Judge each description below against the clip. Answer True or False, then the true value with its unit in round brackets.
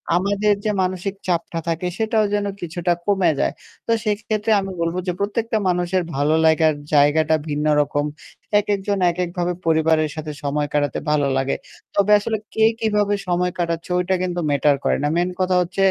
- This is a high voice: False (180 Hz)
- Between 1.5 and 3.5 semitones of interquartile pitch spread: False (4.1 semitones)